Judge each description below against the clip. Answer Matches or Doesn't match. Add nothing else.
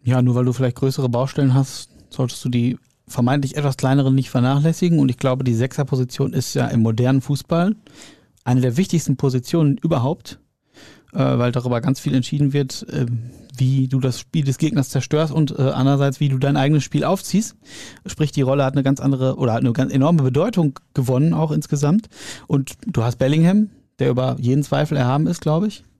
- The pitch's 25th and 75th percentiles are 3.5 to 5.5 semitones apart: Doesn't match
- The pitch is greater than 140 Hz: Doesn't match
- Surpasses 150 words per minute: Matches